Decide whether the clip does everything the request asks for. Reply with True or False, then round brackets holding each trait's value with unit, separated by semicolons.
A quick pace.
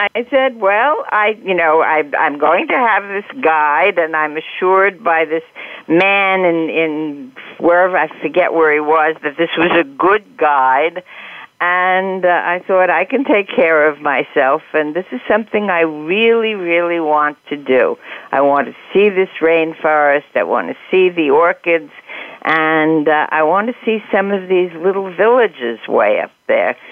False (175 wpm)